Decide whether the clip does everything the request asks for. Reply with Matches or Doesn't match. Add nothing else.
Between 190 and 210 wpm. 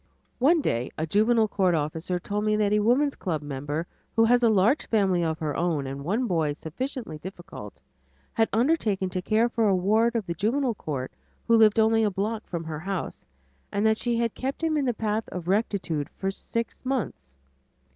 Matches